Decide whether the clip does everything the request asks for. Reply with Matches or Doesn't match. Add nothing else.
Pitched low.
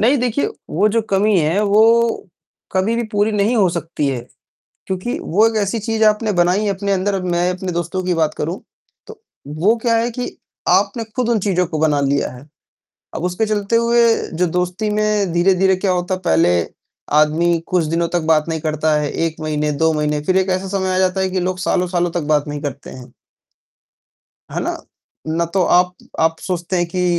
Doesn't match